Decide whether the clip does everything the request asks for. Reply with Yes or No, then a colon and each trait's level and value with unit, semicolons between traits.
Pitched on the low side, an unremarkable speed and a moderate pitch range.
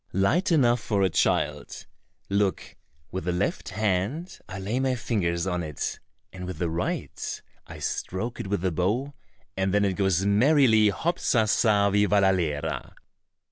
Yes: low, 100 Hz; average, 155 wpm; average, 3.7 semitones